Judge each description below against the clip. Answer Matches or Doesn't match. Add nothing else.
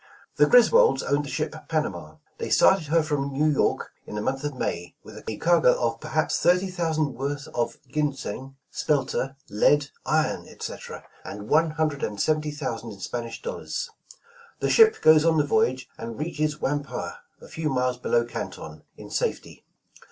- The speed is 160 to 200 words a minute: Matches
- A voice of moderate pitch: Matches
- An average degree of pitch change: Matches